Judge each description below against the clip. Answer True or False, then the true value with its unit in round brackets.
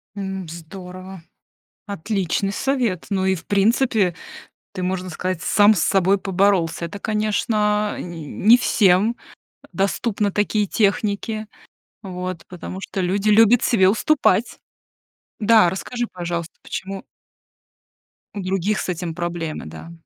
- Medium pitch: False (195 Hz)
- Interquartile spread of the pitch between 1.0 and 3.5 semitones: True (2.7 semitones)